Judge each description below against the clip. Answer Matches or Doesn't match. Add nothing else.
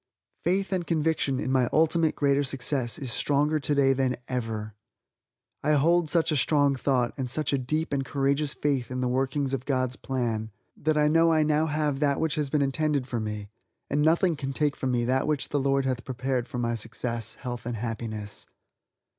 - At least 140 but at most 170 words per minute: Doesn't match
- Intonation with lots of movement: Doesn't match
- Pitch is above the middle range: Doesn't match